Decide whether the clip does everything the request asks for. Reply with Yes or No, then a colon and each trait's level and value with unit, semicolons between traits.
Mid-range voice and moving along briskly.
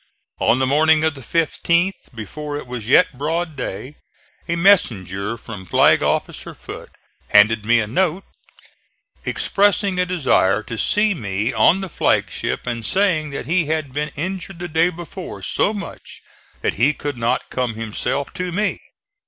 No: medium, 150 Hz; average, 160 wpm